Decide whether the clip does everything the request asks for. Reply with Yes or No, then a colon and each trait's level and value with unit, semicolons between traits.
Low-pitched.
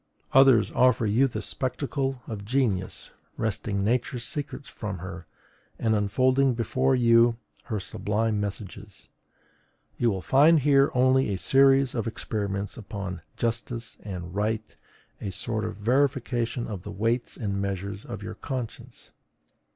Yes: low, 115 Hz